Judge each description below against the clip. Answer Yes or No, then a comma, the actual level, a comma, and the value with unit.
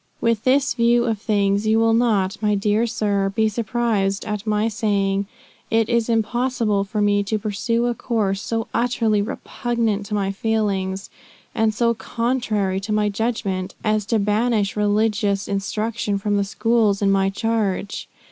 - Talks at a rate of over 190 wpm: No, average, 155 wpm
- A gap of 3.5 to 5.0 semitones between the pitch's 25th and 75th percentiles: No, narrow, 2.4 semitones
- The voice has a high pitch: Yes, high, 215 Hz